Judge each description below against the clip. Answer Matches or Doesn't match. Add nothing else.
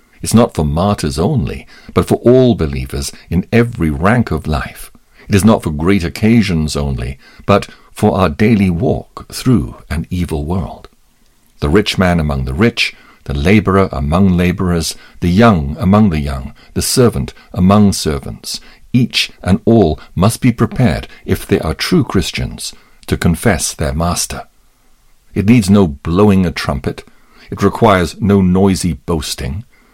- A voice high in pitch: Doesn't match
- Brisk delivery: Doesn't match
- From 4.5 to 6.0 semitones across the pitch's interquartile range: Matches